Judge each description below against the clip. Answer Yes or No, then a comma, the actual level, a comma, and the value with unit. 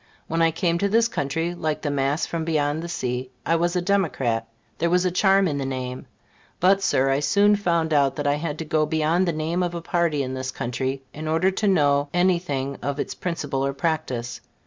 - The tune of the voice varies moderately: Yes, average, 4.0 semitones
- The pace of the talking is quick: Yes, fast, 220 wpm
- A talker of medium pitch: Yes, medium, 155 Hz